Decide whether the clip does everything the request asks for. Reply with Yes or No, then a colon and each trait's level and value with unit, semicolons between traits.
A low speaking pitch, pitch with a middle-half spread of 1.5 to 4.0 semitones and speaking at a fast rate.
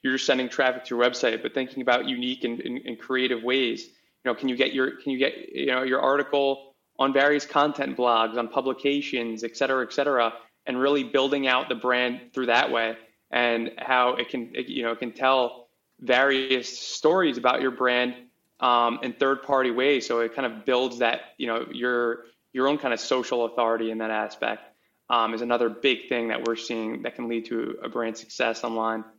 Yes: low, 125 Hz; narrow, 2.4 semitones; fast, 210 wpm